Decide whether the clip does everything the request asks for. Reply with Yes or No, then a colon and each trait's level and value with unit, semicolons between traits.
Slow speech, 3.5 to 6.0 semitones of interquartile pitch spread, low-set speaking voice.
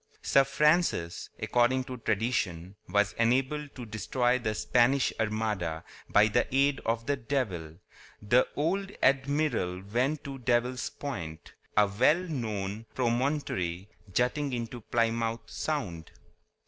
Yes: slow, 120 wpm; average, 4.6 semitones; low, 120 Hz